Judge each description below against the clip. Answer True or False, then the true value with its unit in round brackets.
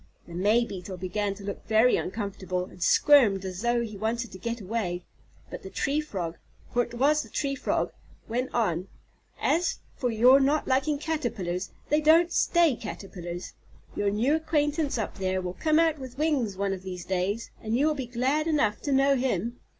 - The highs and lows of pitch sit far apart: True (6.5 semitones)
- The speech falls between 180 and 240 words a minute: True (190 wpm)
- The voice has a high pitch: True (235 Hz)